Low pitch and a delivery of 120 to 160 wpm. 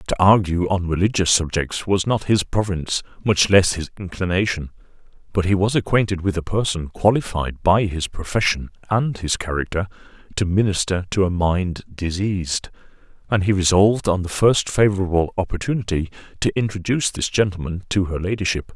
Yes: very low, 95 Hz; average, 155 wpm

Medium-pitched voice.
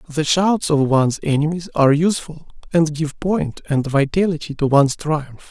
Yes: medium, 155 Hz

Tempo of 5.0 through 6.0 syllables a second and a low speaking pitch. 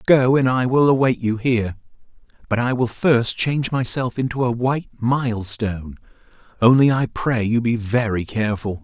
Yes: 5.1 syllables/s; low, 120 Hz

